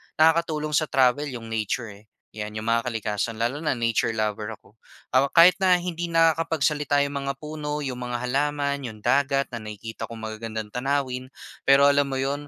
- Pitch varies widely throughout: No, average, 4.6 semitones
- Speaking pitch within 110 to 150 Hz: Yes, low, 135 Hz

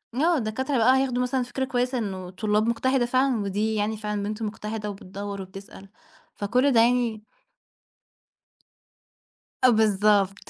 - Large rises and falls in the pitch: No, average, 3.4 semitones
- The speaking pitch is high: Yes, high, 220 Hz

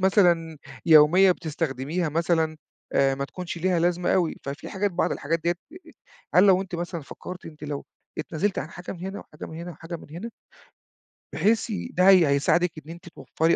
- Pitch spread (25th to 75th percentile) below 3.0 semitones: Yes, narrow, 2.5 semitones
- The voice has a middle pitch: Yes, medium, 170 Hz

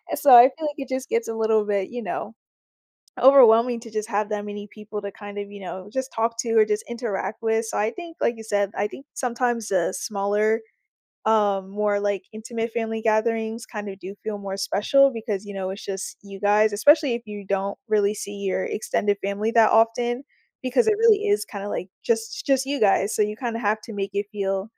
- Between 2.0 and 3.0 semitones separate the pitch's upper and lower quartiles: Yes, narrow, 2.4 semitones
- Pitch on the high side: Yes, high, 215 Hz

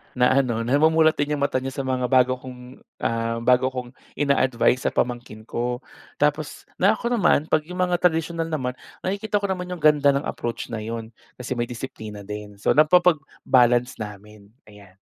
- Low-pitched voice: Yes, low, 130 Hz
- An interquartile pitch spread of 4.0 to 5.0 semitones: Yes, average, 4.5 semitones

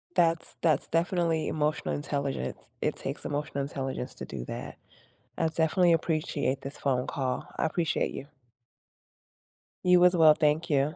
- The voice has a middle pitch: Yes, medium, 155 Hz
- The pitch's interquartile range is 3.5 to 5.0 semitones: No, average, 2.9 semitones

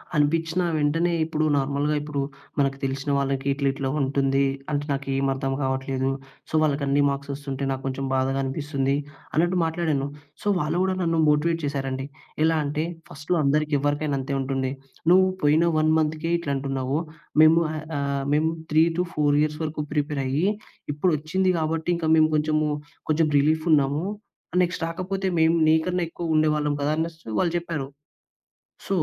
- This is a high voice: No, medium, 150 Hz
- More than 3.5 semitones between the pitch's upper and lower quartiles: No, average, 2.8 semitones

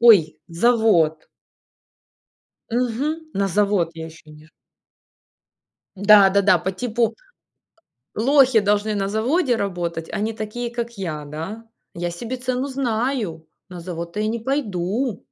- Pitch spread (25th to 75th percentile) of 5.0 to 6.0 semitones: Yes, wide, 5.5 semitones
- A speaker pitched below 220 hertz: Yes, high, 210 Hz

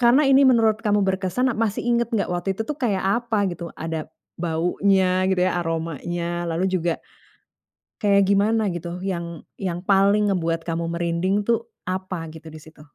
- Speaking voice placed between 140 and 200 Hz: Yes, medium, 185 Hz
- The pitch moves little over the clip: No, average, 3.5 semitones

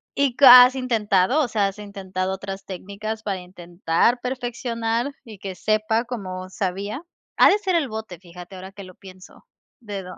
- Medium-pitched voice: No, high, 205 Hz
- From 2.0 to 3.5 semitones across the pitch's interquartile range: No, average, 4.2 semitones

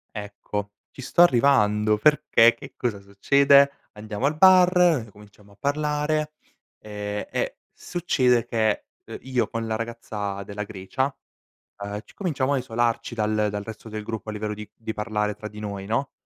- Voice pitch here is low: Yes, low, 110 Hz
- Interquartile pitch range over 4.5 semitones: Yes, average, 4.9 semitones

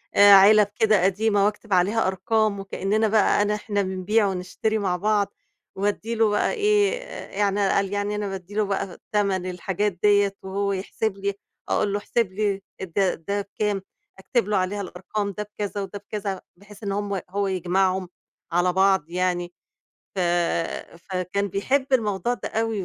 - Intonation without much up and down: Yes, narrow, 1.7 semitones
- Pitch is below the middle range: No, high, 200 Hz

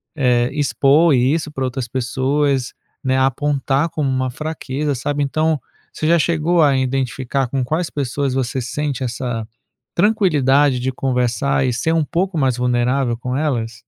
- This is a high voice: No, low, 135 Hz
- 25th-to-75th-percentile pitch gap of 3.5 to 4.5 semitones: No, average, 2.9 semitones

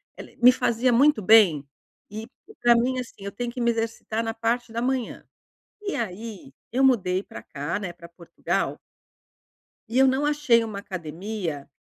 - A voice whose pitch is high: Yes, high, 225 Hz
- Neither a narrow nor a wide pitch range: Yes, average, 4.6 semitones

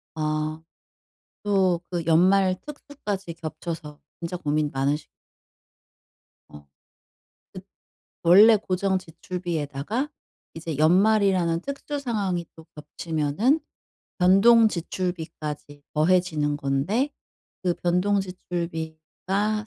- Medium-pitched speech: Yes, medium, 175 Hz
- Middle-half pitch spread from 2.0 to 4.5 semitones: Yes, average, 4.0 semitones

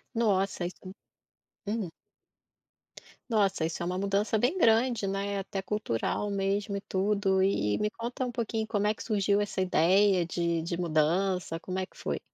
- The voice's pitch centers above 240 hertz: No, high, 195 Hz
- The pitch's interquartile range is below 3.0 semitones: Yes, narrow, 2.4 semitones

